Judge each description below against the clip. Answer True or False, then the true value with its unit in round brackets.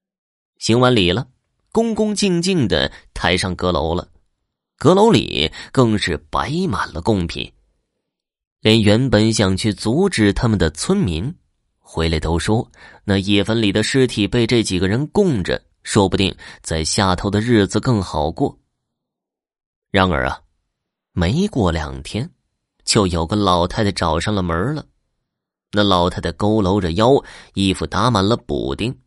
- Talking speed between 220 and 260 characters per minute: False (205 characters per minute)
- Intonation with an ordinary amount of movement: True (4.7 semitones)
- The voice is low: True (105 Hz)